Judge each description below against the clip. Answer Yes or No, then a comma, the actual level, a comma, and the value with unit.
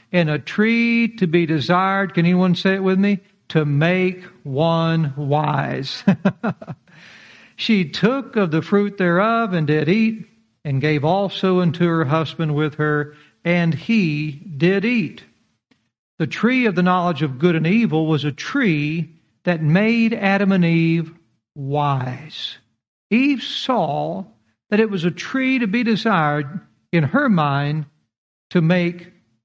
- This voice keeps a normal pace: Yes, average, 145 wpm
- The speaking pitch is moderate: Yes, medium, 175 Hz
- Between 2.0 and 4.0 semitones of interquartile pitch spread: No, average, 4.7 semitones